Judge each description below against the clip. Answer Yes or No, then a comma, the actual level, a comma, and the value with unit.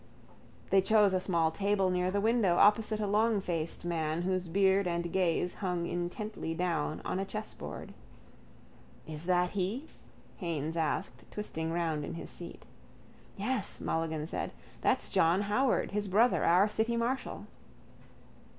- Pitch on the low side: No, medium, 185 Hz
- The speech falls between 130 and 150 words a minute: Yes, average, 140 wpm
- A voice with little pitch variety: No, average, 3.6 semitones